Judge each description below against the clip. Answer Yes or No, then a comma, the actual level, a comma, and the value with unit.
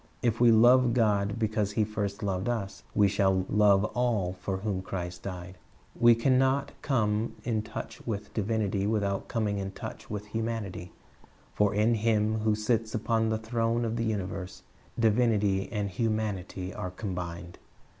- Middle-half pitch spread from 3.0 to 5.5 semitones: No, narrow, 2.5 semitones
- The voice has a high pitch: No, low, 105 Hz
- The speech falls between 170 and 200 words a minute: No, average, 155 wpm